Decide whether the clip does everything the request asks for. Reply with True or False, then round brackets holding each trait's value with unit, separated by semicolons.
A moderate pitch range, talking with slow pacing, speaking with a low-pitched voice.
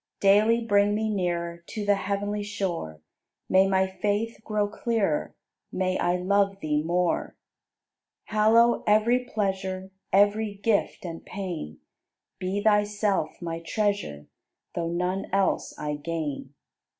False (3.0 semitones; 120 wpm; 195 Hz)